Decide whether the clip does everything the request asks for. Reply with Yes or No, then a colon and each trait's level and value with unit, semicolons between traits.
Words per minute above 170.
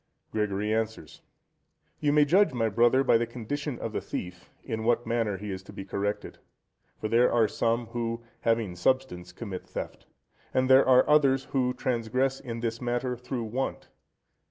No: average, 165 wpm